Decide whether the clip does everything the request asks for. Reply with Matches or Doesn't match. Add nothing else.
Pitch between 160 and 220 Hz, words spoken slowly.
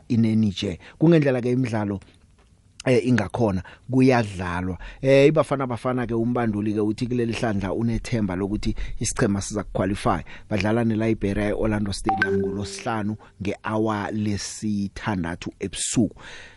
Doesn't match